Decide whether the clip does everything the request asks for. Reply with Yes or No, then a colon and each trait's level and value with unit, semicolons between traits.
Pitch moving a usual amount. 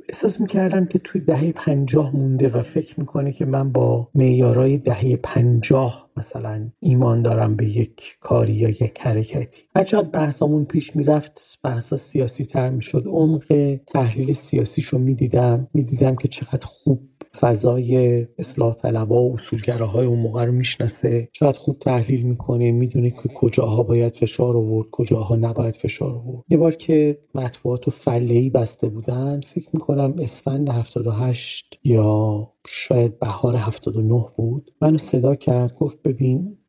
Yes: average, 3.4 semitones